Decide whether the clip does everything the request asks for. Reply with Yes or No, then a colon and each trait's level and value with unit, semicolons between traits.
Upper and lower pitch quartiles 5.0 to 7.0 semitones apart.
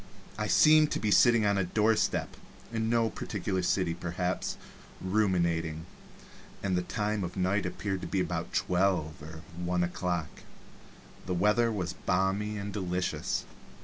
No: average, 3.0 semitones